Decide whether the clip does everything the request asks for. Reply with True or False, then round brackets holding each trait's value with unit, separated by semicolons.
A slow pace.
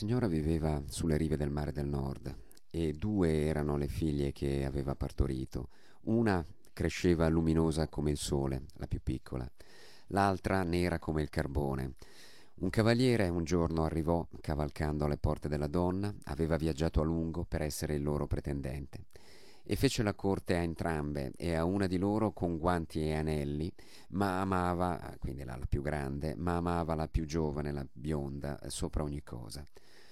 False (160 wpm)